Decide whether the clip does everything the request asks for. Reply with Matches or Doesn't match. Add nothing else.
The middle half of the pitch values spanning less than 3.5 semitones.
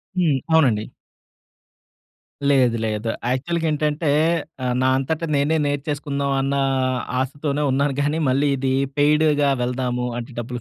Matches